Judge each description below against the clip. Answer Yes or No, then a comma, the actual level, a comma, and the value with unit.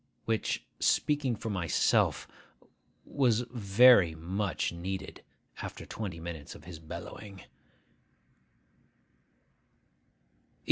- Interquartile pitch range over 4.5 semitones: Yes, average, 4.9 semitones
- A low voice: Yes, very low, 95 Hz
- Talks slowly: Yes, slow, 80 wpm